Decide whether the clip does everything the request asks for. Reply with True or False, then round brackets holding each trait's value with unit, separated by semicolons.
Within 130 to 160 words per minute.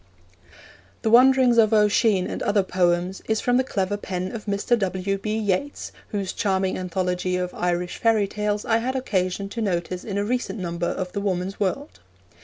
False (180 wpm)